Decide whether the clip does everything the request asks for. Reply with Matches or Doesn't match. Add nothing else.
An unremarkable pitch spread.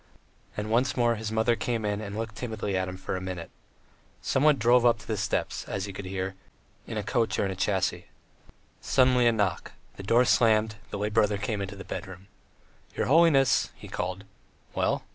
Matches